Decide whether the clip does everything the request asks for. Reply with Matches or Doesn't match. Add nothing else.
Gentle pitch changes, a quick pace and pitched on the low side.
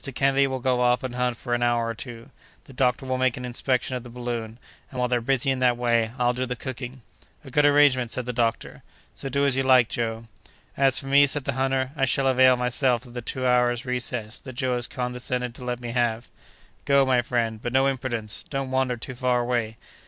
Matches